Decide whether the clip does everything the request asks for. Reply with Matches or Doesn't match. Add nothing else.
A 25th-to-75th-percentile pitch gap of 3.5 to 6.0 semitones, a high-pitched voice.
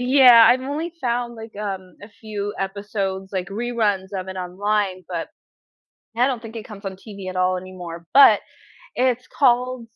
Matches